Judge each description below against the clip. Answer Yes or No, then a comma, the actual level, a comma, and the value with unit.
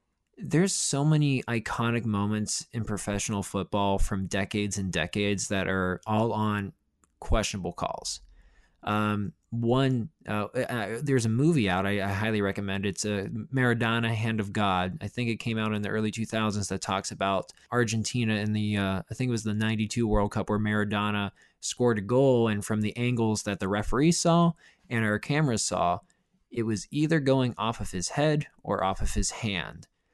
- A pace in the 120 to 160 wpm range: No, average, 180 wpm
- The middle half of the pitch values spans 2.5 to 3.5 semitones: Yes, average, 2.9 semitones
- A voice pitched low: Yes, low, 110 Hz